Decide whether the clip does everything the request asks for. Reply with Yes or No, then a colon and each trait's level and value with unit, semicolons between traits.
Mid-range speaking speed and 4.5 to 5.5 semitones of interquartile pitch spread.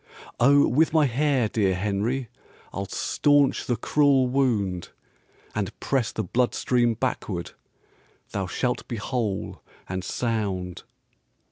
No: slow, 120 wpm; average, 5.1 semitones